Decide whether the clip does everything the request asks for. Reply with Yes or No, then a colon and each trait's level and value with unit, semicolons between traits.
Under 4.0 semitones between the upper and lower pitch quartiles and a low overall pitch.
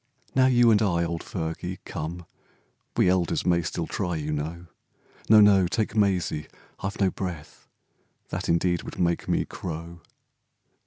Yes: average, 2.8 semitones; very low, 90 Hz